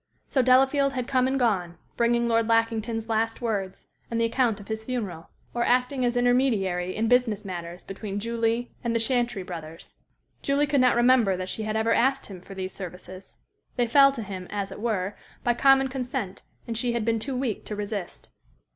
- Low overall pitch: No, high, 230 Hz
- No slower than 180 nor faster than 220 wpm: Yes, average, 195 wpm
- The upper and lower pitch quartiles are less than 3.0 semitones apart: No, average, 4.0 semitones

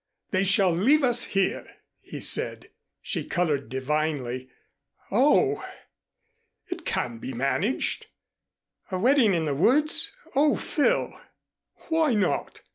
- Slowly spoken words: Yes, slow, 115 wpm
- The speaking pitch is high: Yes, high, 195 Hz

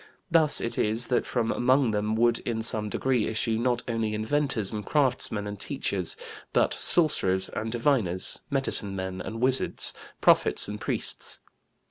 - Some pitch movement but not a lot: Yes, average, 3.3 semitones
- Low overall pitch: Yes, low, 115 Hz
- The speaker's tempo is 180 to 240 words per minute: No, average, 150 wpm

